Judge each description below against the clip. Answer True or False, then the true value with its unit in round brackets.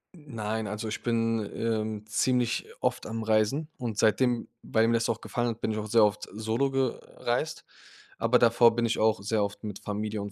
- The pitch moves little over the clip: True (1.7 semitones)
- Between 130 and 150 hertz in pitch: False (110 Hz)